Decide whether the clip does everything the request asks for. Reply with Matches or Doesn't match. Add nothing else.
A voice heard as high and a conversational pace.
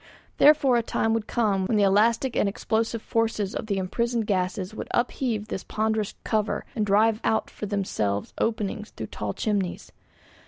Matches